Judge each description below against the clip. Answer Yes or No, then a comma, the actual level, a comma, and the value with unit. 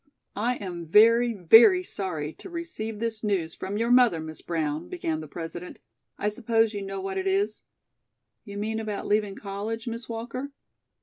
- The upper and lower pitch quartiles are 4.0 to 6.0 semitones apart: No, average, 3.6 semitones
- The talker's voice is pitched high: Yes, high, 210 Hz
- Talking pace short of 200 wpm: Yes, average, 170 wpm